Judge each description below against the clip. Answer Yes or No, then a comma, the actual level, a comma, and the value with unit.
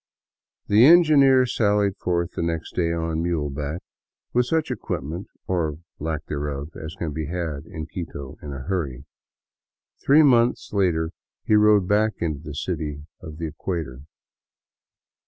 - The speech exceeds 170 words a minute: No, average, 145 wpm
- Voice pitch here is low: Yes, very low, 85 Hz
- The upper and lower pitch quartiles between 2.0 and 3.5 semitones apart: No, average, 5.3 semitones